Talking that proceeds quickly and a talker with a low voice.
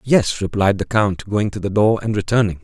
Yes: fast, 225 wpm; low, 105 Hz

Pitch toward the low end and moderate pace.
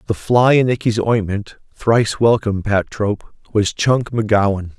Yes: low, 110 Hz; average, 150 wpm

